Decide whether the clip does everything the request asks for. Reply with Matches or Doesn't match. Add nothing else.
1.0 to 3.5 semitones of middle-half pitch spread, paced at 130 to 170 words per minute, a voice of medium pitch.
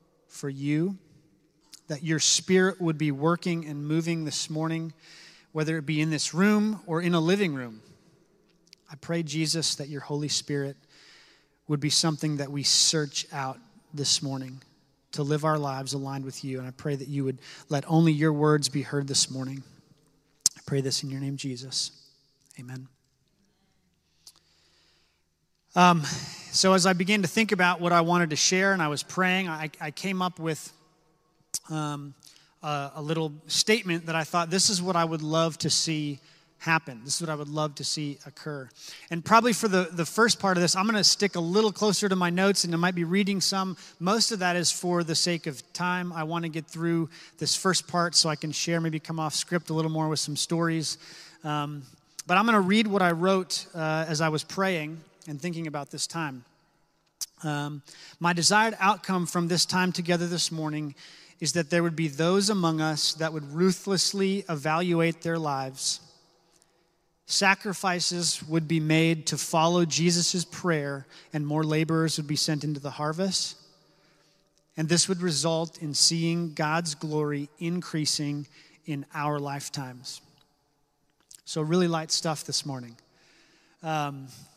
Doesn't match